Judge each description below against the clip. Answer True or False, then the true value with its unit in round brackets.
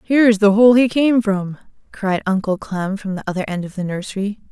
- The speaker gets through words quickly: True (225 wpm)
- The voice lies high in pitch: True (205 Hz)